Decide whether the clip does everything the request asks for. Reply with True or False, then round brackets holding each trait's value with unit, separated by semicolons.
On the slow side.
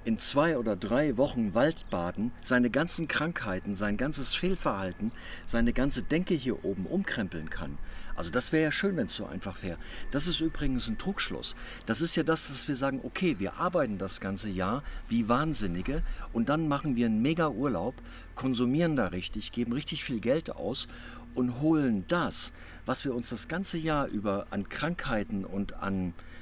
False (175 wpm)